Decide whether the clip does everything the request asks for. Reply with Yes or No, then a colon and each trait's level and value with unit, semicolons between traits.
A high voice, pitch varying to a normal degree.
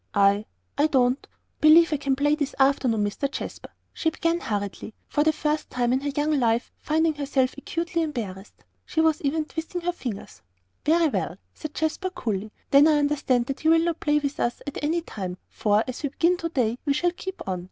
Yes: very high, 290 Hz; average, 4.5 semitones